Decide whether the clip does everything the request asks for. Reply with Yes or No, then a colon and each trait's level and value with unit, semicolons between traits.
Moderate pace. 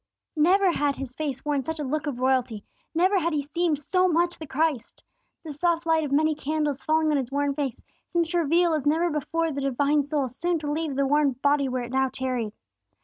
No: fast, 220 wpm